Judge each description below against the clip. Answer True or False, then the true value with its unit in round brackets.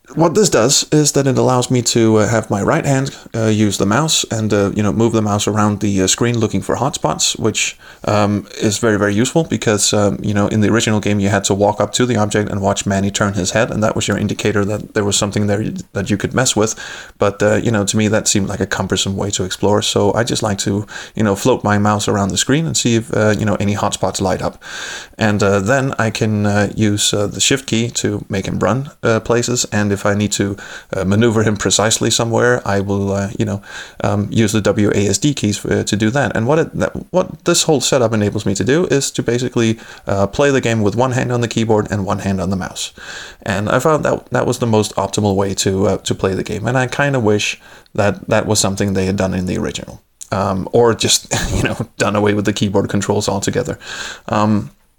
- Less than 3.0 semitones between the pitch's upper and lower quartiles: True (2.5 semitones)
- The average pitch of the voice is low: True (105 Hz)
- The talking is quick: True (250 wpm)